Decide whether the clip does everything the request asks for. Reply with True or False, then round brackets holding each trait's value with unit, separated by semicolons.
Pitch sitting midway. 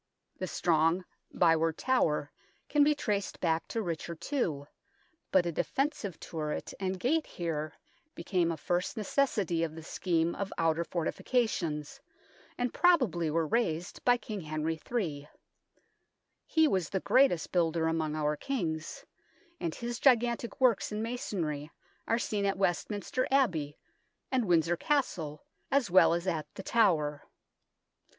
True (175 Hz)